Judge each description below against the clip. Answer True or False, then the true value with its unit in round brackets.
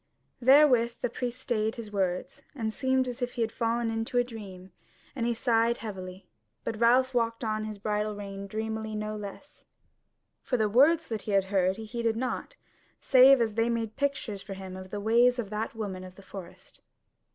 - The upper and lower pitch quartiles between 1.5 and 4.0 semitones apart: True (2.9 semitones)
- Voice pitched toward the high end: True (225 Hz)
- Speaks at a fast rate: False (195 wpm)